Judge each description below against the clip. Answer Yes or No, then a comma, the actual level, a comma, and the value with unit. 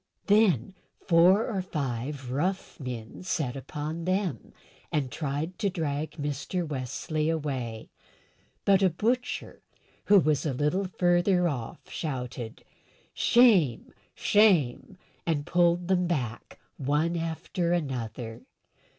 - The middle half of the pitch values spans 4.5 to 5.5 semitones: Yes, average, 5.2 semitones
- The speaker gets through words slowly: Yes, slow, 110 wpm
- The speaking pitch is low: No, medium, 160 Hz